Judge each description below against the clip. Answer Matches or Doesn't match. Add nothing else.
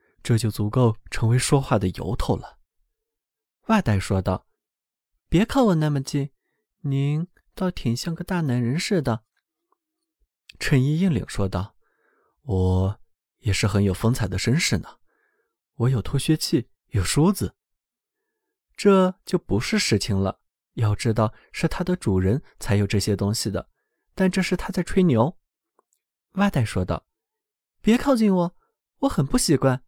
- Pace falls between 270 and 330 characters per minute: Doesn't match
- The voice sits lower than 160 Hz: Matches